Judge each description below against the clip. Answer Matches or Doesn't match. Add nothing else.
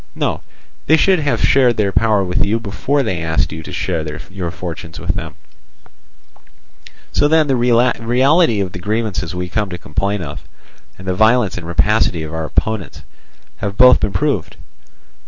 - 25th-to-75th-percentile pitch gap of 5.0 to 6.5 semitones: Matches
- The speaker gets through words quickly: Doesn't match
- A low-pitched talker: Matches